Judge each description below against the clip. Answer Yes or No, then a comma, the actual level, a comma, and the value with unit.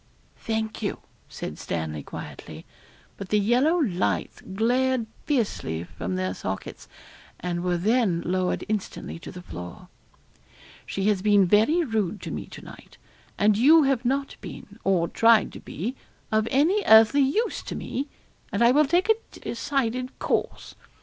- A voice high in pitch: Yes, high, 220 Hz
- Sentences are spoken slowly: No, average, 150 wpm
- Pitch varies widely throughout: Yes, wide, 6.2 semitones